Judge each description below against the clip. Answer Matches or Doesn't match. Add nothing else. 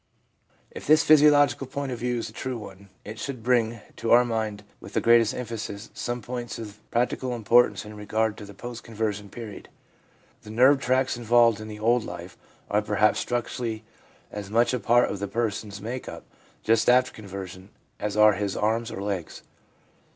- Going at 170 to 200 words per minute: Matches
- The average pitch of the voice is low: Matches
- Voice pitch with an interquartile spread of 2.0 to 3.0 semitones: Matches